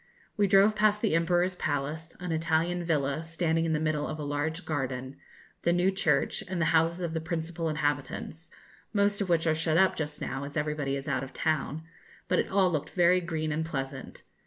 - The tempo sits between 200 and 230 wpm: Yes, fast, 205 wpm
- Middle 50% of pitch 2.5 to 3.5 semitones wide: Yes, average, 2.8 semitones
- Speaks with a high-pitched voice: No, medium, 160 Hz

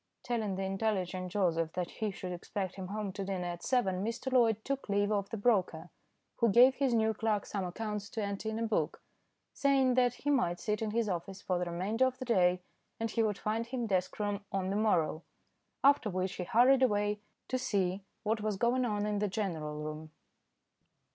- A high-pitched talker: Yes, high, 205 Hz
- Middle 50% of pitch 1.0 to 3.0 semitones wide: No, average, 3.6 semitones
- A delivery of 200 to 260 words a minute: Yes, fast, 205 wpm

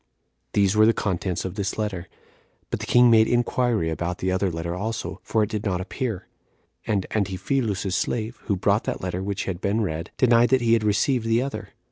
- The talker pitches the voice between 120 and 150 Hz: No, low, 105 Hz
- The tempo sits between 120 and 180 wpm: No, average, 200 wpm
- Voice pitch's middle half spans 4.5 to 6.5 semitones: No, average, 3.5 semitones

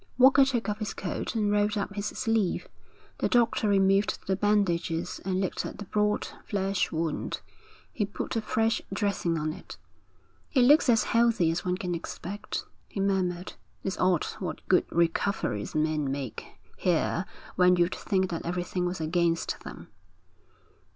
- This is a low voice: No, high, 190 Hz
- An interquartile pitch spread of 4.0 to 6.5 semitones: No, average, 3.3 semitones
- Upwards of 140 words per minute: Yes, average, 155 wpm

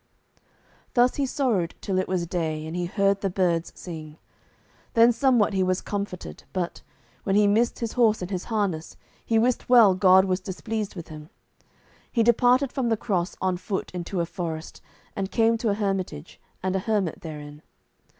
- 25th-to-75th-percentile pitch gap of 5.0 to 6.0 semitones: No, average, 4.2 semitones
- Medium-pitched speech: No, high, 195 Hz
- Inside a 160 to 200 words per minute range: Yes, average, 180 wpm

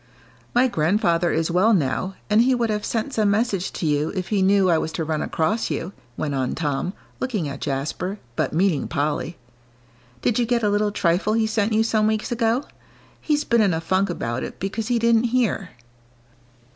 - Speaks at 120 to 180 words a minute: No, average, 195 wpm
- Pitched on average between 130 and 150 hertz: No, high, 200 Hz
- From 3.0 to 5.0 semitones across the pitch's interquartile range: No, wide, 5.4 semitones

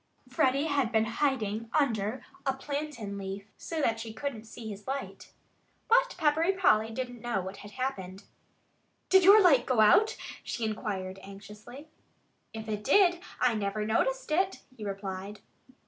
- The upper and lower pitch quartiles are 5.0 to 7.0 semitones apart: Yes, wide, 5.5 semitones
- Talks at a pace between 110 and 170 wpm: Yes, average, 150 wpm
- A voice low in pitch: No, high, 230 Hz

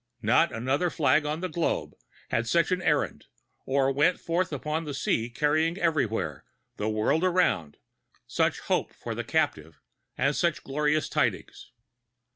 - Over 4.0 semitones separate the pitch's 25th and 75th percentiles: Yes, average, 4.7 semitones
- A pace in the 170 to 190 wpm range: No, average, 145 wpm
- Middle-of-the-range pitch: Yes, medium, 150 Hz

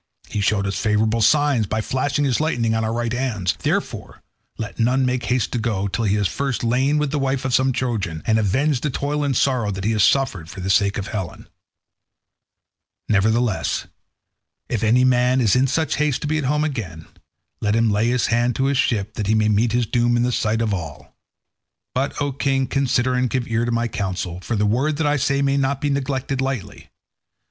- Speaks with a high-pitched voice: No, low, 120 Hz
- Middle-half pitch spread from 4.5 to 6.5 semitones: No, average, 4.0 semitones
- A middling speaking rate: No, fast, 215 wpm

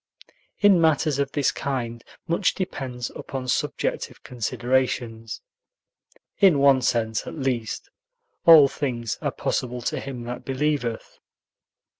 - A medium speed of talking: No, slow, 115 wpm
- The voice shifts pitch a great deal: No, average, 3.4 semitones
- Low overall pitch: Yes, low, 130 Hz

